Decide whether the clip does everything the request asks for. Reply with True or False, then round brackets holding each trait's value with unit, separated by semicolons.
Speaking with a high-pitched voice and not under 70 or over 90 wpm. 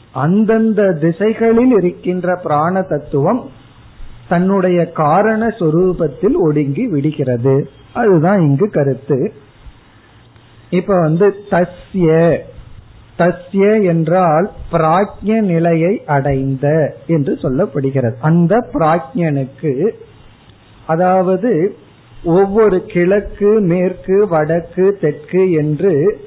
False (170 Hz; 75 wpm)